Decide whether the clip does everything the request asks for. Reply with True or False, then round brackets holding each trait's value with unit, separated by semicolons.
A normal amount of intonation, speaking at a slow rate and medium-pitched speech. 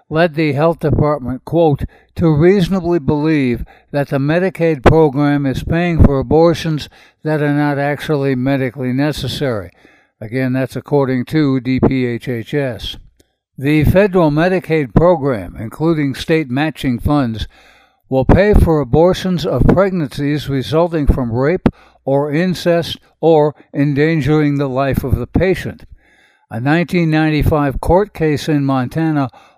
True (3.5 semitones; 120 wpm; 145 Hz)